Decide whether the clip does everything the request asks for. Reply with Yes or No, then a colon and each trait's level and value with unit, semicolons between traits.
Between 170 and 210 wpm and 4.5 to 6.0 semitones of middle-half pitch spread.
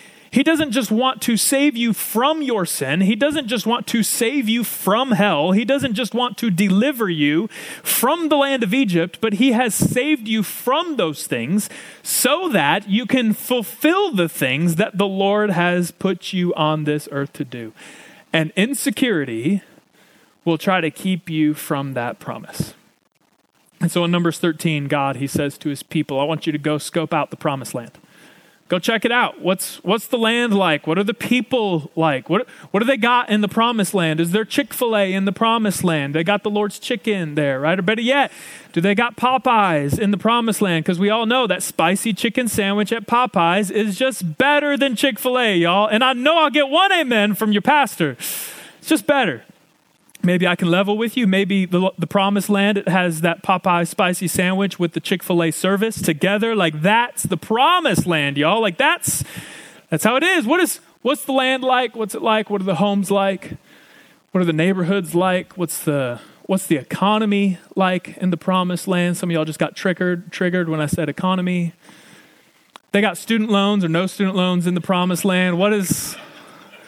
Yes: average, 200 wpm; average, 5.2 semitones